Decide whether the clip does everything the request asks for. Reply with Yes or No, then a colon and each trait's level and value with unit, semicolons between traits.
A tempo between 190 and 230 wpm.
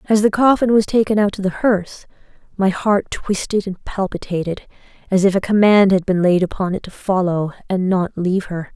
Yes: average, 200 wpm